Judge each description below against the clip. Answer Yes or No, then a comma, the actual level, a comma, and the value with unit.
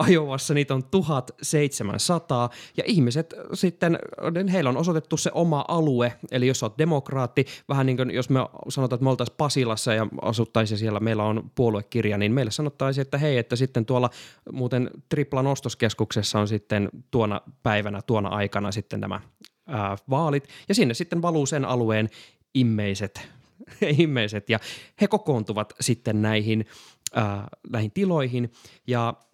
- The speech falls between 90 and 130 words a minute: No, average, 145 wpm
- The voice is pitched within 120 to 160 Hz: Yes, low, 125 Hz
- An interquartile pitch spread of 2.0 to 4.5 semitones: No, average, 4.9 semitones